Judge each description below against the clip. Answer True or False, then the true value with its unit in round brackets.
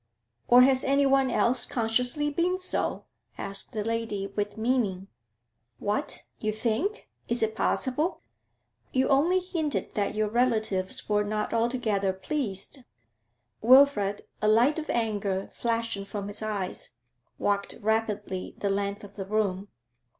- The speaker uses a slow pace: True (130 wpm)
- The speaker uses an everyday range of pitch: True (4.1 semitones)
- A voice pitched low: False (220 Hz)